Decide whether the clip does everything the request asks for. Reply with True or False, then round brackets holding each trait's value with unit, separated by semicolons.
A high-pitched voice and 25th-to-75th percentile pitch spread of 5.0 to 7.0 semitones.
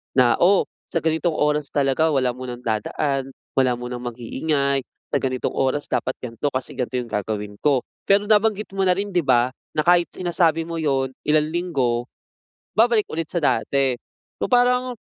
False (145 Hz; 5.4 semitones)